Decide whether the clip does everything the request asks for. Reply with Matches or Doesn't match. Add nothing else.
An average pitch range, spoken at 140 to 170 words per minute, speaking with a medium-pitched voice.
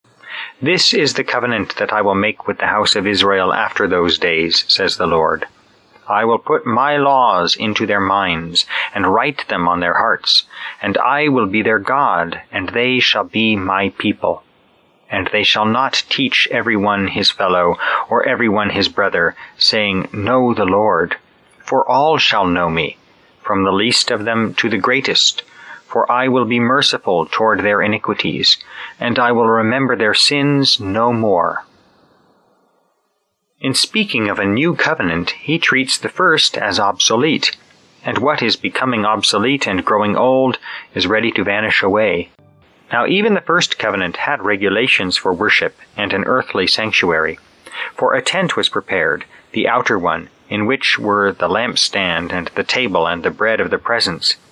Doesn't match